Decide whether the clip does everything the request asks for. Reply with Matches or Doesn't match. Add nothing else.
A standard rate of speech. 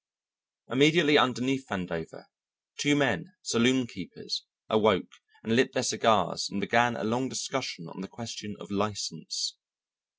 Doesn't match